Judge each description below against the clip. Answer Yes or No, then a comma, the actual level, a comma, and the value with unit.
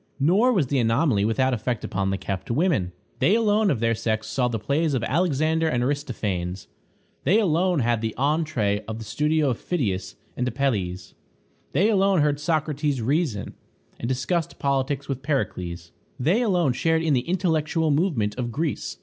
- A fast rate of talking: No, average, 165 wpm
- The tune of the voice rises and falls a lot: Yes, wide, 6.1 semitones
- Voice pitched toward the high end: No, medium, 140 Hz